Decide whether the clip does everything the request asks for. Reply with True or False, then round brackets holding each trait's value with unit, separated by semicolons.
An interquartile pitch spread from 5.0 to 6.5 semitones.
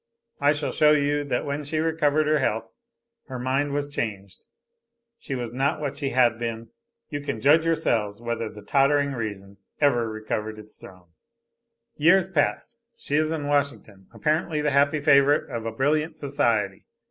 False (4.6 semitones)